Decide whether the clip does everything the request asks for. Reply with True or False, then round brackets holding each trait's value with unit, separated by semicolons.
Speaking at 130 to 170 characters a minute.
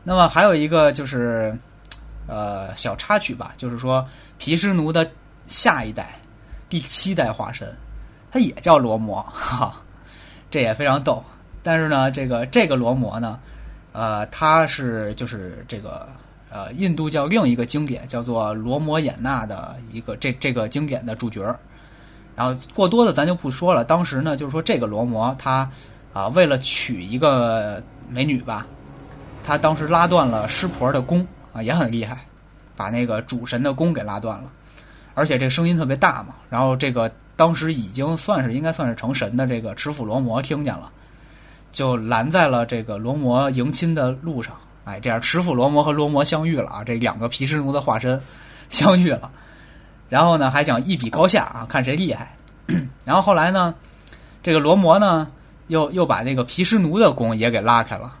False (260 characters per minute)